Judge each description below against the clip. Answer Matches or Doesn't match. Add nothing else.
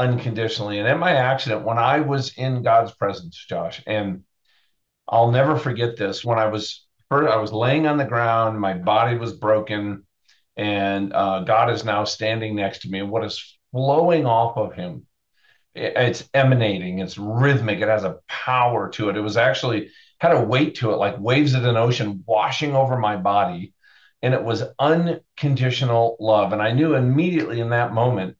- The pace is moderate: Matches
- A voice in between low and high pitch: Doesn't match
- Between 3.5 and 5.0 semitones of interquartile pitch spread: Matches